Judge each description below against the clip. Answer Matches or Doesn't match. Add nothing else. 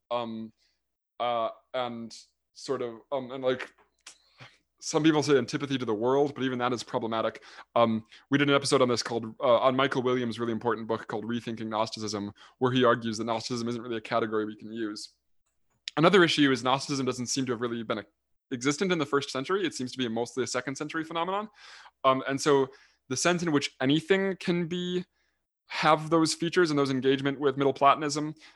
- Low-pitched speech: Matches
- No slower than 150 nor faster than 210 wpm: Matches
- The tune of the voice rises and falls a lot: Doesn't match